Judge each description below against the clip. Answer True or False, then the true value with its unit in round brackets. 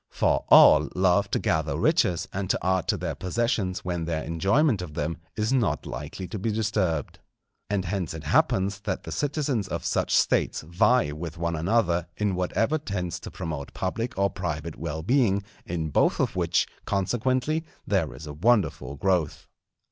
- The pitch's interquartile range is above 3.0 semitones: True (4.4 semitones)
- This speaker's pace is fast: False (170 wpm)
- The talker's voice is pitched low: True (95 Hz)